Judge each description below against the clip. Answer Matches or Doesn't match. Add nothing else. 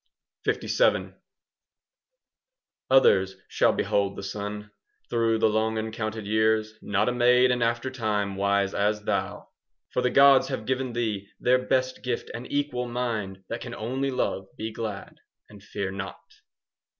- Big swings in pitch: Doesn't match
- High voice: Doesn't match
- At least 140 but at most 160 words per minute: Matches